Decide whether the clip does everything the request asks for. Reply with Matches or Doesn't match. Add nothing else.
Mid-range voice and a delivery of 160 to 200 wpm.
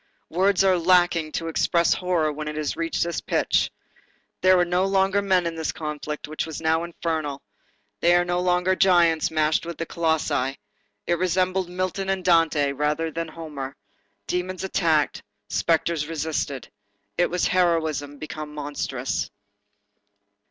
Doesn't match